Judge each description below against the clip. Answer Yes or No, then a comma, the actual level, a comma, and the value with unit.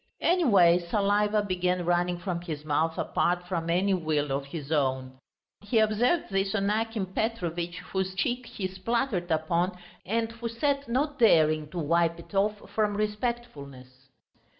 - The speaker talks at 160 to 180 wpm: No, average, 150 wpm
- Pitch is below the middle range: No, medium, 185 Hz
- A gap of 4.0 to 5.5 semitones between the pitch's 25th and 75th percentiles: Yes, average, 4.6 semitones